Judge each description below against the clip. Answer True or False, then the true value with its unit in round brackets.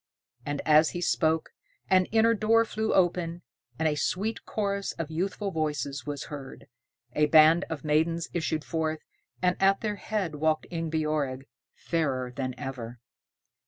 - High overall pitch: False (160 Hz)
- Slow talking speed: False (145 wpm)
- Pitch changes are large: False (3.8 semitones)